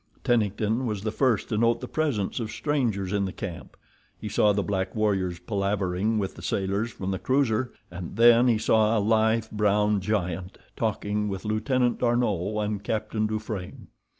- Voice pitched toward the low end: Yes, low, 105 Hz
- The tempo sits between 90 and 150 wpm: No, average, 170 wpm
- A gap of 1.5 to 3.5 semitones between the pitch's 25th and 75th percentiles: Yes, narrow, 2.6 semitones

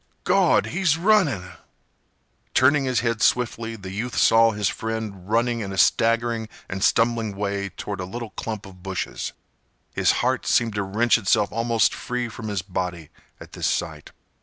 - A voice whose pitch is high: No, low, 110 Hz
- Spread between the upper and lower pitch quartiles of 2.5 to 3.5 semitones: Yes, average, 3.0 semitones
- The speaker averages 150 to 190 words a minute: Yes, average, 160 wpm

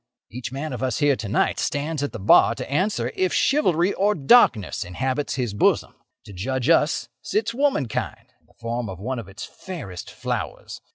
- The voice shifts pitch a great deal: Yes, wide, 6.3 semitones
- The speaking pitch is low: Yes, low, 130 Hz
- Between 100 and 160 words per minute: No, average, 185 wpm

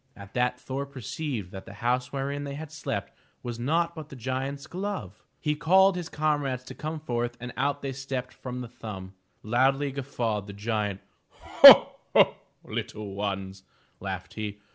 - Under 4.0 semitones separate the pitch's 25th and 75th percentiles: No, average, 5.1 semitones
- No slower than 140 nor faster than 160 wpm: No, average, 170 wpm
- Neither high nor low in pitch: No, low, 125 Hz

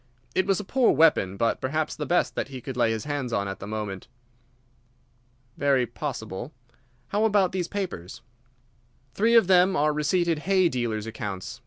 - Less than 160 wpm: No, average, 170 wpm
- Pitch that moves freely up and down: Yes, wide, 8.5 semitones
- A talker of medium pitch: Yes, medium, 145 Hz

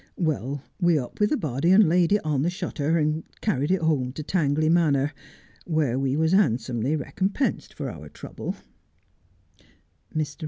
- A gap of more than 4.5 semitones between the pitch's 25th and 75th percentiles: No, average, 3.9 semitones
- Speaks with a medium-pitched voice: Yes, medium, 155 Hz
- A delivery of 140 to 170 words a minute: Yes, average, 155 wpm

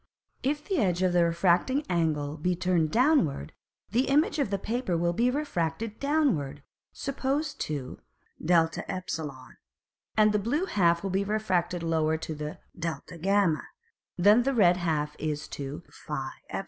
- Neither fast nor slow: Yes, average, 150 wpm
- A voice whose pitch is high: No, medium, 180 Hz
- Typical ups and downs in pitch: No, wide, 6.8 semitones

